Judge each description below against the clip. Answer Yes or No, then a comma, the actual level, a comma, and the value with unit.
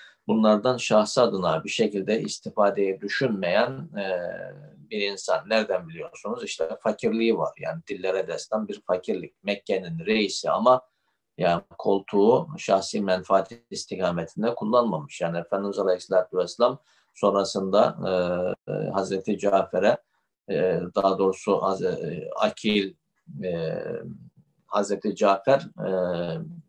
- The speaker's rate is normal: No, slow, 90 wpm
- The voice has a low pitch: Yes, low, 100 Hz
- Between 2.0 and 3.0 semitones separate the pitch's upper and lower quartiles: Yes, average, 2.7 semitones